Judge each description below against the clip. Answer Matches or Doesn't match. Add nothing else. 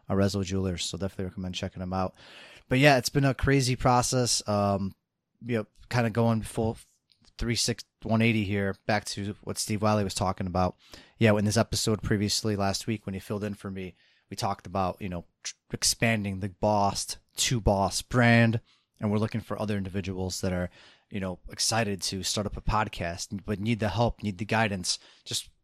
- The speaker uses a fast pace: Doesn't match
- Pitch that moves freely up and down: Doesn't match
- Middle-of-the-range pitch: Doesn't match